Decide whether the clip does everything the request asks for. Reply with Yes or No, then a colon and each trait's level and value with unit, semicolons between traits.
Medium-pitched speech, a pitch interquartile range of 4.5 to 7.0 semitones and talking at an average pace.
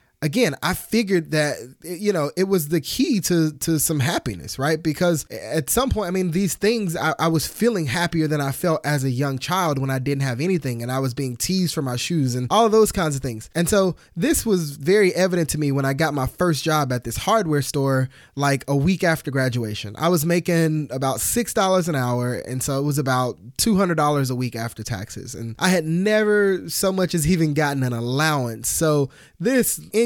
No: medium, 155 Hz; average, 5.2 semitones; fast, 225 wpm